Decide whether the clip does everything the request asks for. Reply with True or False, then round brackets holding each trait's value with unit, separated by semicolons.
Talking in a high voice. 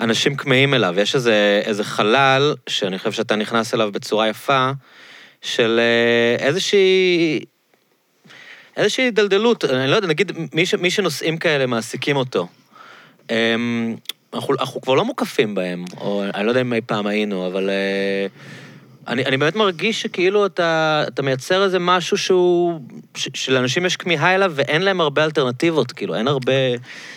False (135 Hz)